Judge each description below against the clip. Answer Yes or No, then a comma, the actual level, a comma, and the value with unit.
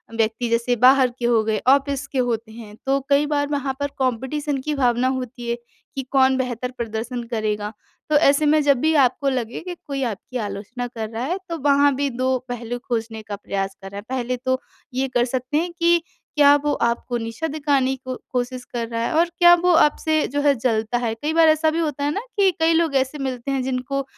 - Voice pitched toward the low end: No, very high, 260 Hz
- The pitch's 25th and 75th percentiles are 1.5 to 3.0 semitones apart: No, average, 3.4 semitones